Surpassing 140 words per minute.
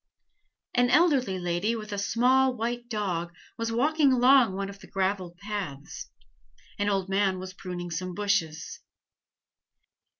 No: slow, 135 wpm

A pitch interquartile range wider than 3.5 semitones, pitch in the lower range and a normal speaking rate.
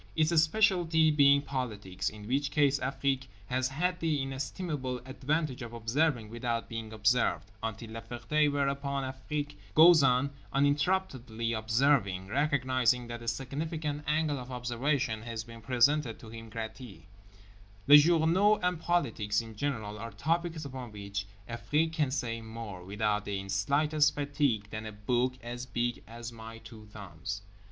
Yes: average, 4.5 semitones; low, 125 Hz; average, 145 wpm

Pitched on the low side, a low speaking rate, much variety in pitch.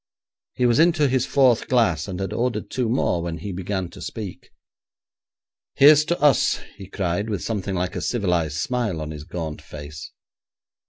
No: low, 100 Hz; average, 170 wpm; wide, 6.4 semitones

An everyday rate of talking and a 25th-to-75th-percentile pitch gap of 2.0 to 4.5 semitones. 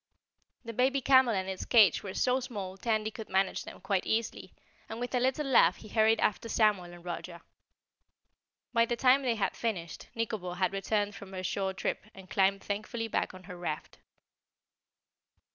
Yes: average, 180 wpm; average, 3.6 semitones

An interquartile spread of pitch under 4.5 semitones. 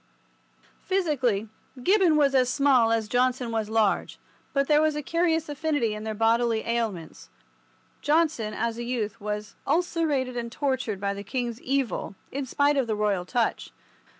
No: average, 4.8 semitones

